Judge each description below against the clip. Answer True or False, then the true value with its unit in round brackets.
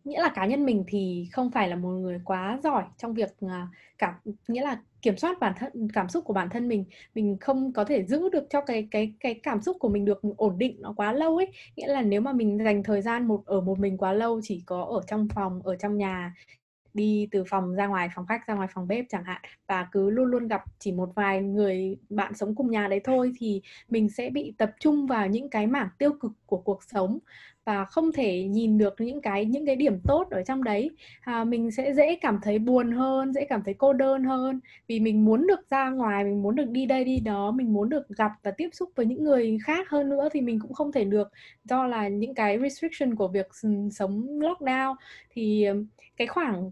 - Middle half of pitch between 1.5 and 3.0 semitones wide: False (4.6 semitones)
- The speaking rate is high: False (240 wpm)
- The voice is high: True (220 Hz)